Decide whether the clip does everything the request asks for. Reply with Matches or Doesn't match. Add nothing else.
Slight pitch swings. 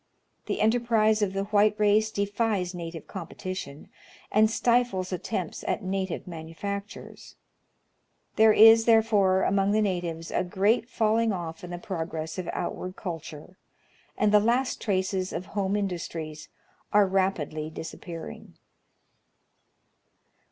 Doesn't match